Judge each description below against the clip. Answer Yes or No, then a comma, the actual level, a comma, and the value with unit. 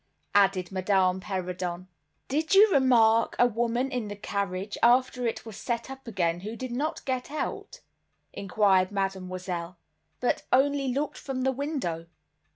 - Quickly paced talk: No, average, 145 wpm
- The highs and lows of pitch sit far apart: Yes, wide, 5.7 semitones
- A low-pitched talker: No, high, 220 Hz